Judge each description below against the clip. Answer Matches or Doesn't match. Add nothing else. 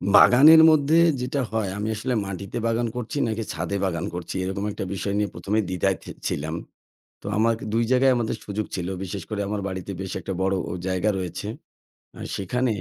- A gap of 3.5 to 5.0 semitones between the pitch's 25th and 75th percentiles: Matches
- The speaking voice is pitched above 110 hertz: Doesn't match